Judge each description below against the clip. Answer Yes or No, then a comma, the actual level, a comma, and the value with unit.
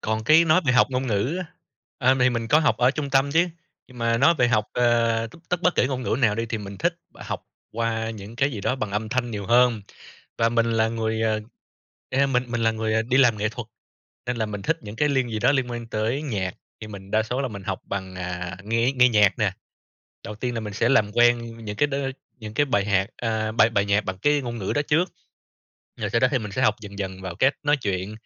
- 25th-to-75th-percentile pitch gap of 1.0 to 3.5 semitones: Yes, average, 3.1 semitones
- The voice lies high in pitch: No, low, 115 Hz